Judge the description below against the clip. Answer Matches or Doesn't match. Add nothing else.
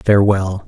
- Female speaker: Doesn't match